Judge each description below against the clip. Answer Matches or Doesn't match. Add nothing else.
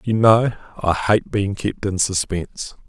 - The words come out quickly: Doesn't match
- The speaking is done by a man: Matches